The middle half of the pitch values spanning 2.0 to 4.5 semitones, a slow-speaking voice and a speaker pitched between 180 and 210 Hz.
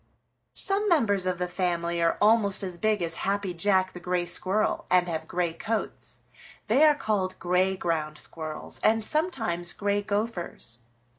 No: average, 3.6 semitones; average, 155 wpm; medium, 185 Hz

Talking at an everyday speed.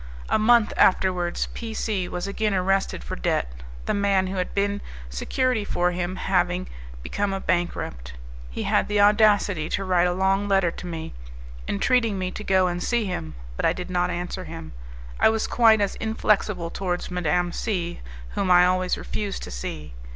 Yes: average, 180 wpm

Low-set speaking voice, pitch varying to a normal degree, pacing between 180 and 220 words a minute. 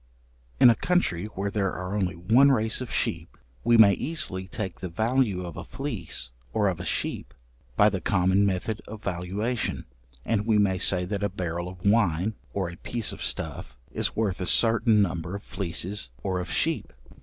Yes: low, 100 Hz; average, 3.4 semitones; average, 190 wpm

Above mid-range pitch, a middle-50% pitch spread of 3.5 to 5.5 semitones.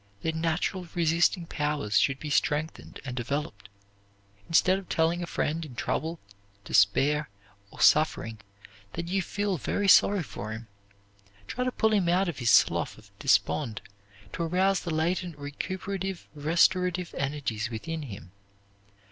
No: medium, 160 Hz; average, 4.4 semitones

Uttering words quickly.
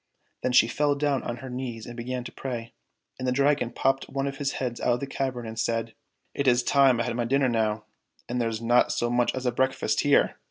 Yes: fast, 240 wpm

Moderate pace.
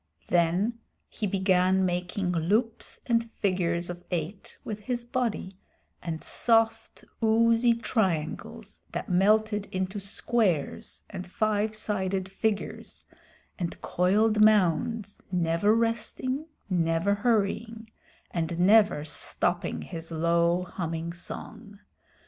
No: slow, 100 wpm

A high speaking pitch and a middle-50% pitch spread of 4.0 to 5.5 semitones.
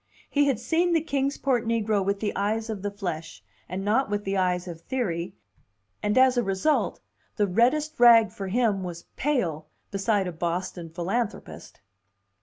Yes: high, 205 Hz; average, 4.8 semitones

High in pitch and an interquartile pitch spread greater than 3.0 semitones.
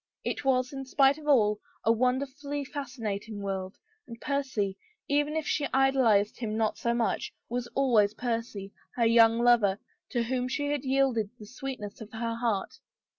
Yes: high, 240 Hz; average, 3.8 semitones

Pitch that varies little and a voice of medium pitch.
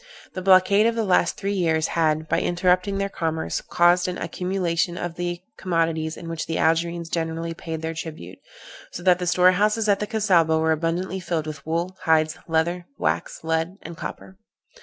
Yes: narrow, 2.2 semitones; medium, 170 Hz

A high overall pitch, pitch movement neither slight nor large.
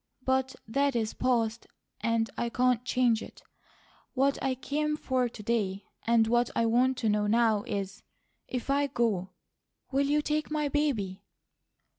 Yes: high, 240 Hz; average, 3.4 semitones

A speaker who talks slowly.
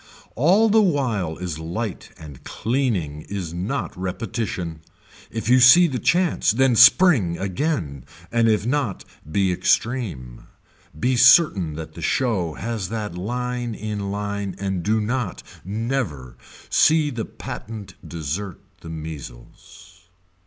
Yes: slow, 125 wpm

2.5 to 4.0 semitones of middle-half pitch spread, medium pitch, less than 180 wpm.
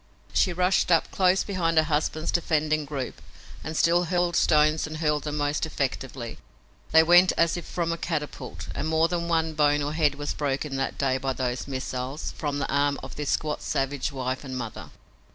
No: average, 2.9 semitones; medium, 150 Hz; average, 190 wpm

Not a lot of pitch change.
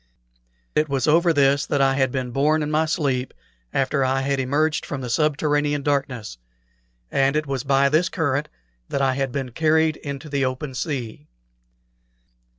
Yes: narrow, 2.2 semitones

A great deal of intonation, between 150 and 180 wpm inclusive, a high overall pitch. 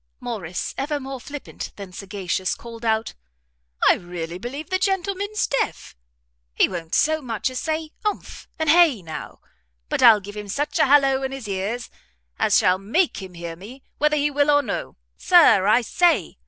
Yes: wide, 7.3 semitones; average, 175 wpm; very high, 250 Hz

